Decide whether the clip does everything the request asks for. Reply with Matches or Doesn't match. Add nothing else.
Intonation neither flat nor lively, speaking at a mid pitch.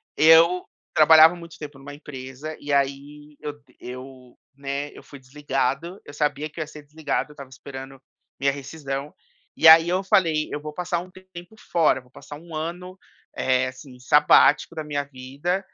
Matches